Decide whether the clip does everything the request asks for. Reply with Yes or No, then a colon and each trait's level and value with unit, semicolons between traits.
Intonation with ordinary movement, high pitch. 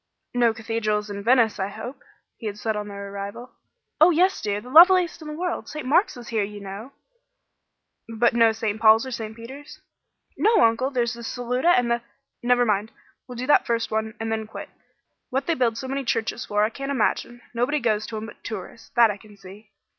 Yes: average, 3.2 semitones; high, 230 Hz